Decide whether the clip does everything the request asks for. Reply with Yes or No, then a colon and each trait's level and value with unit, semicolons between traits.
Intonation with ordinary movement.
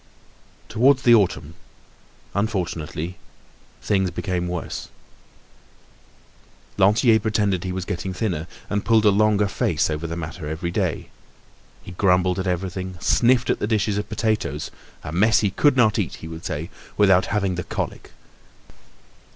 Yes: average, 3.4 semitones